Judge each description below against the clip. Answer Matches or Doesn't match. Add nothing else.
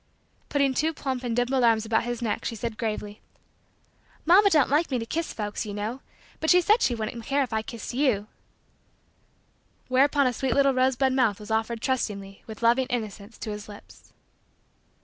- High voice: Matches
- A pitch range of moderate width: Matches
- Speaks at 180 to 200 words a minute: Matches